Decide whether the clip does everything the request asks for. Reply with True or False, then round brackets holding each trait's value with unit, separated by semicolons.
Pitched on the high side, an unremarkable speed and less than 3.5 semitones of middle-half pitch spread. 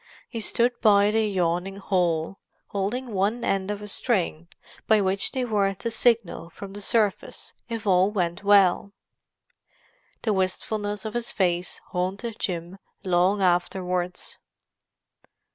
False (195 Hz; 130 wpm; 2.8 semitones)